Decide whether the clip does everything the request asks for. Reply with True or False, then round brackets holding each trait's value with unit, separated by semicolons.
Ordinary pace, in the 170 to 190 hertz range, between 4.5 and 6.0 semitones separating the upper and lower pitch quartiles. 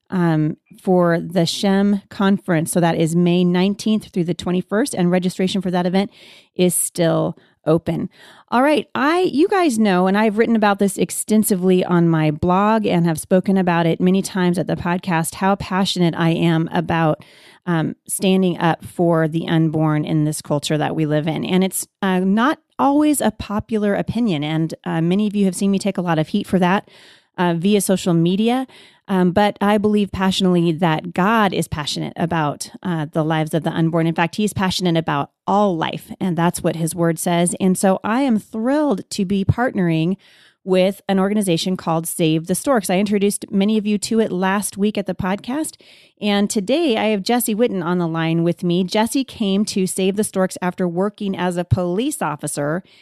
False (195 wpm; 185 Hz; 3.4 semitones)